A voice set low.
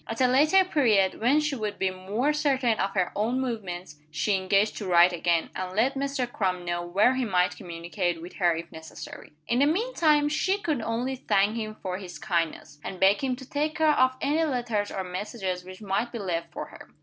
No: high, 215 Hz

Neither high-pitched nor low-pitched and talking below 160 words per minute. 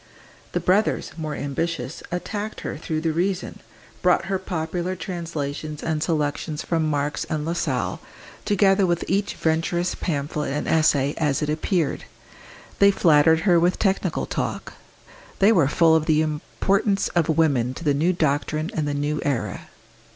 Yes: medium, 160 Hz; average, 150 wpm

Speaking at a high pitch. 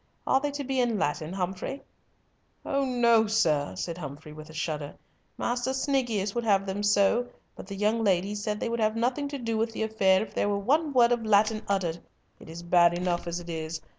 Yes: high, 205 Hz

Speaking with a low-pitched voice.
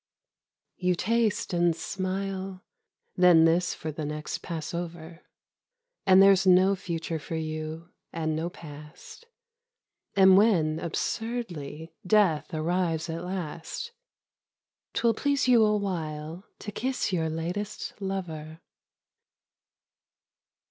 No: medium, 175 Hz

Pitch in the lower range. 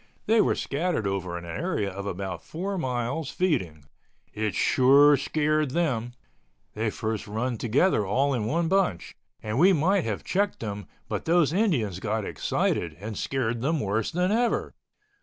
Yes: low, 125 Hz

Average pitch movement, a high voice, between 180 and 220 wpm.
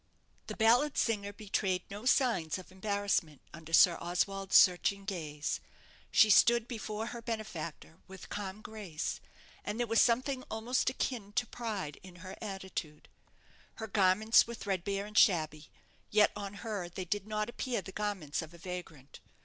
No: average, 3.6 semitones; high, 200 Hz; average, 155 wpm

